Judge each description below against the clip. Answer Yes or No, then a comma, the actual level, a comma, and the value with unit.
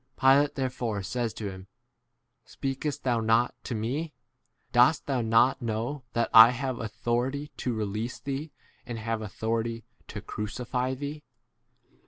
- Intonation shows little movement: No, average, 3.0 semitones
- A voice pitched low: Yes, low, 120 Hz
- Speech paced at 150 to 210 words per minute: No, average, 140 wpm